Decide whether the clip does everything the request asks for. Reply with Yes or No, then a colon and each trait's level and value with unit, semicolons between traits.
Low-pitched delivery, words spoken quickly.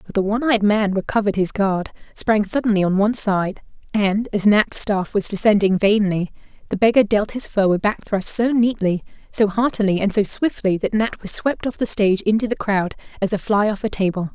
No: high, 205 Hz; fast, 215 wpm